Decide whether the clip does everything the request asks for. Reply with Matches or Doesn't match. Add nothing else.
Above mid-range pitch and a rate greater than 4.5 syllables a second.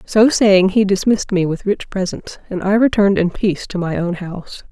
Matches